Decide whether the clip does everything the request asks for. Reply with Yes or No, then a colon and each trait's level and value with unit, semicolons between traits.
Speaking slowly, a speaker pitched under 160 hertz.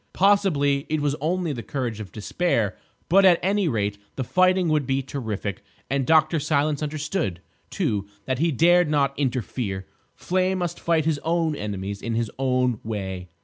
No: average, 165 wpm; medium, 140 Hz